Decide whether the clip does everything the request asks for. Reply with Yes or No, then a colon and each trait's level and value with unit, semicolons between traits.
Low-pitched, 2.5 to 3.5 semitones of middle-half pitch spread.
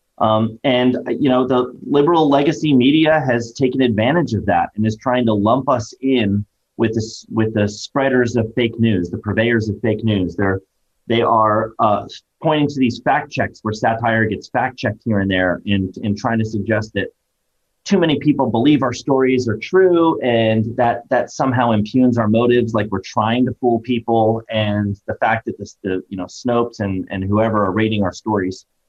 Yes: low, 115 Hz; average, 3.2 semitones